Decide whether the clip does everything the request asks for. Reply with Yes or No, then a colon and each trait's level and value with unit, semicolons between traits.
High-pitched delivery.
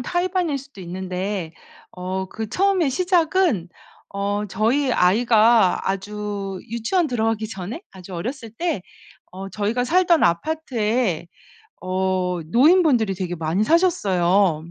Yes: high, 210 Hz